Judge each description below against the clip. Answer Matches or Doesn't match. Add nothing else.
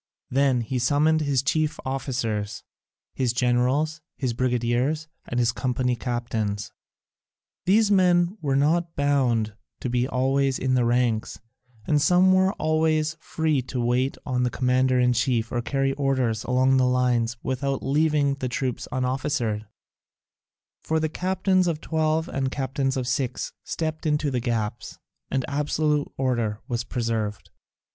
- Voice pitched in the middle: Doesn't match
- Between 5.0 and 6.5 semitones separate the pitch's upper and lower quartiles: Doesn't match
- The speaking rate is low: Doesn't match